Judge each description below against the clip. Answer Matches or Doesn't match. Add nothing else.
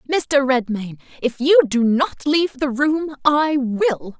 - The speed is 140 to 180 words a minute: Matches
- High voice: Matches